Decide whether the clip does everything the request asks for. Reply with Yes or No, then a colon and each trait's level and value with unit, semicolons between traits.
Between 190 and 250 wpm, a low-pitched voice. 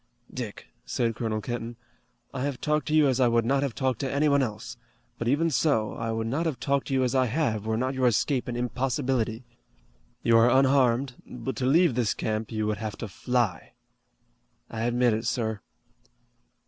Yes: average, 195 wpm; low, 125 Hz